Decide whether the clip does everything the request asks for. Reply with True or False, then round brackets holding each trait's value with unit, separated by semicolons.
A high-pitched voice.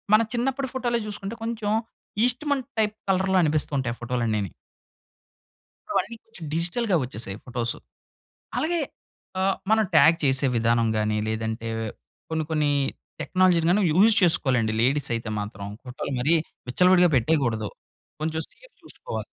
False (160 Hz)